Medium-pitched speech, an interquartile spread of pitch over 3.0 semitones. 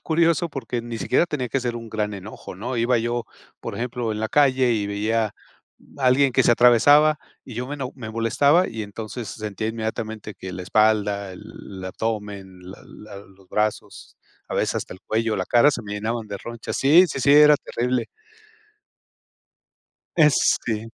No: low, 115 Hz; average, 3.4 semitones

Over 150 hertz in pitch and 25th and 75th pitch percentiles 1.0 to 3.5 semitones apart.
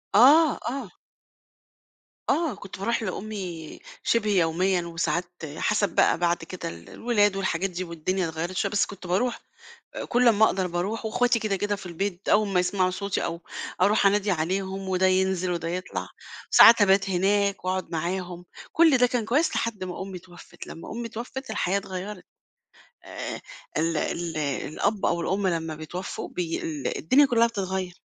Yes: high, 190 Hz; average, 3.2 semitones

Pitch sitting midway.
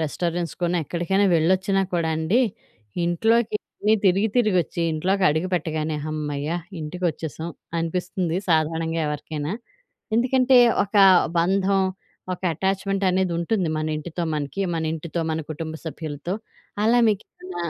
Yes: medium, 175 Hz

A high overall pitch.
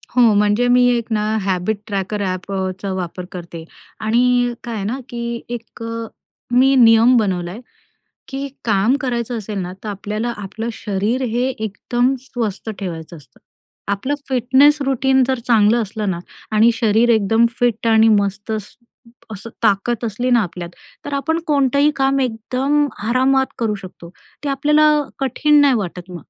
Yes: high, 230 Hz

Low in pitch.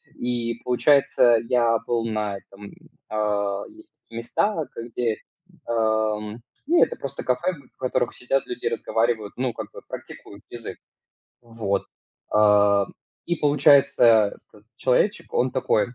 Yes: low, 115 Hz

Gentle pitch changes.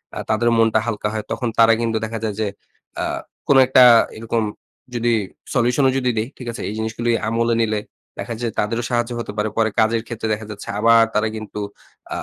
Yes: narrow, 1.3 semitones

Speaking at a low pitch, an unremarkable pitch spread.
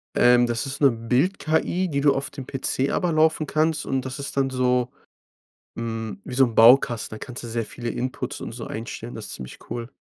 Yes: low, 125 Hz; average, 3.0 semitones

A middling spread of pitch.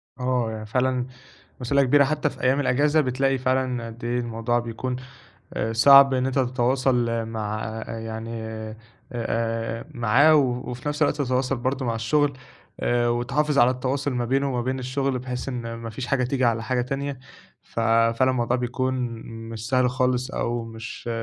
No: narrow, 2.3 semitones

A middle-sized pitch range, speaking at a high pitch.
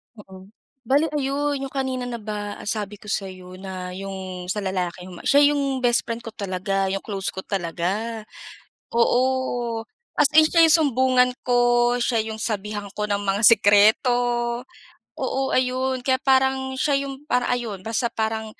Yes: average, 4.8 semitones; high, 230 Hz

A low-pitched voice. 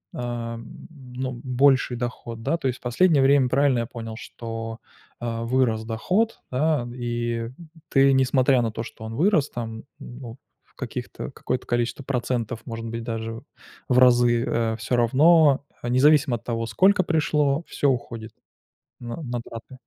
Yes: low, 120 Hz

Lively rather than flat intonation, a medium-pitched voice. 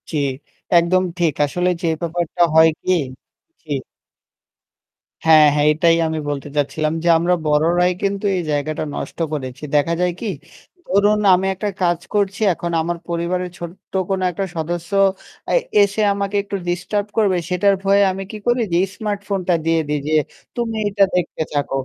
No: average, 3.6 semitones; medium, 175 Hz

